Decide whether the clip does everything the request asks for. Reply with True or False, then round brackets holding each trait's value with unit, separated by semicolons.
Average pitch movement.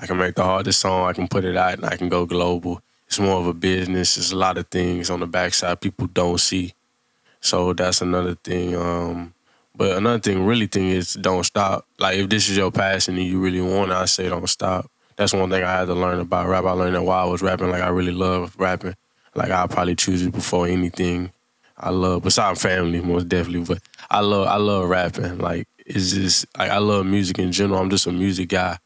False (1.2 semitones)